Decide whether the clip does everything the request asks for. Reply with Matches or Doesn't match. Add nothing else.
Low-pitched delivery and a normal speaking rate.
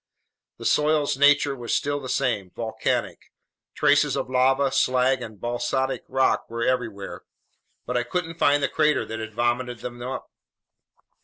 Matches